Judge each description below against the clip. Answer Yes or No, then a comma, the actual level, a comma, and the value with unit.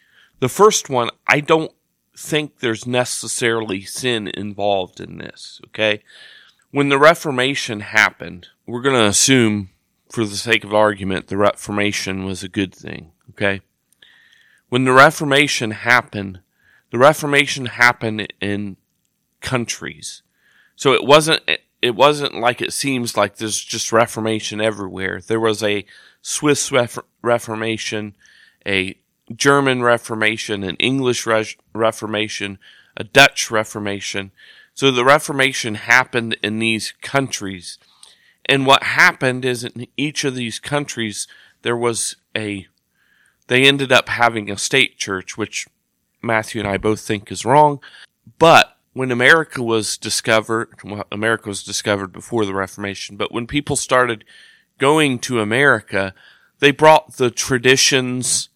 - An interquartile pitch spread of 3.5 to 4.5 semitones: Yes, average, 4.0 semitones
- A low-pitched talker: Yes, low, 115 Hz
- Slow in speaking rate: Yes, slow, 130 wpm